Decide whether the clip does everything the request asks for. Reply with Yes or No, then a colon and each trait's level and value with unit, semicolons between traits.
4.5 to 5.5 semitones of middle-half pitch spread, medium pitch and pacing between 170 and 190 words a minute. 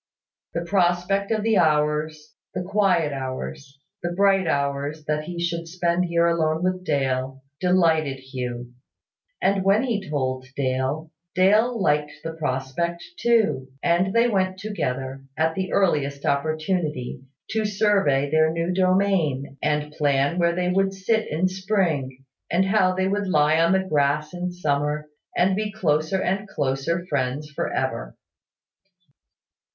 No: average, 4.8 semitones; medium, 165 Hz; average, 140 wpm